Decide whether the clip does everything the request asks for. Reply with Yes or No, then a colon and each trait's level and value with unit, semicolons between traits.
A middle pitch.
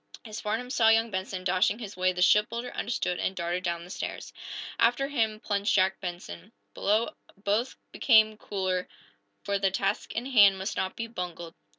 No: high, 200 Hz